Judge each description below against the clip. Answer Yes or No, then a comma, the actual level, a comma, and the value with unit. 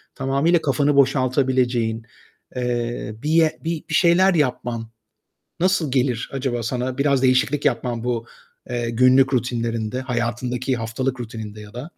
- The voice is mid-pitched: No, low, 125 Hz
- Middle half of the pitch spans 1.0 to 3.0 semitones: Yes, narrow, 2.6 semitones